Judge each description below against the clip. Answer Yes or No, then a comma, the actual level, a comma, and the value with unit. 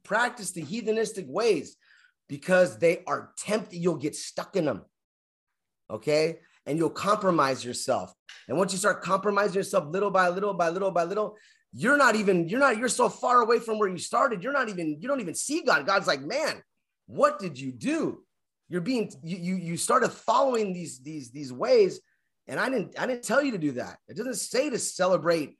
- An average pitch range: No, wide, 6.3 semitones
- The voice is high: Yes, high, 195 Hz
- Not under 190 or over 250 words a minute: Yes, average, 200 wpm